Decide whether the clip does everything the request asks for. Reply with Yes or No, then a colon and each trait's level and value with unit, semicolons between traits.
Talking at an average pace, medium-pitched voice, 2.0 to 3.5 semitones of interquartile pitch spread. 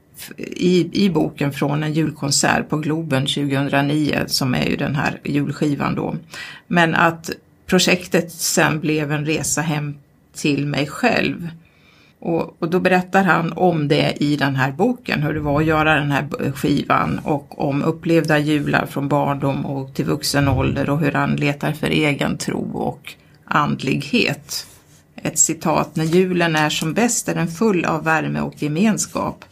Yes: average, 160 wpm; medium, 155 Hz; average, 2.9 semitones